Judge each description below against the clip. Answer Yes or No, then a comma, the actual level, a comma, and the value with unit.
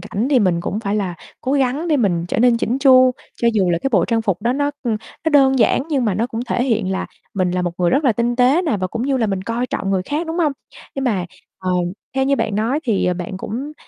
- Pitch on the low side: No, high, 230 Hz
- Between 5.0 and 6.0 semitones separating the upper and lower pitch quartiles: Yes, wide, 5.4 semitones